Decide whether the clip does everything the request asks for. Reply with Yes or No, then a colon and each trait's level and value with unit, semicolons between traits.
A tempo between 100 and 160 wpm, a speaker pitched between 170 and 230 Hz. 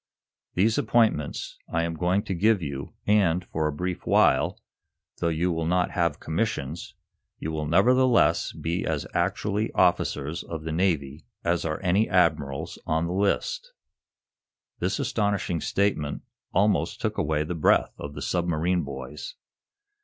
No: average, 140 wpm; very low, 85 Hz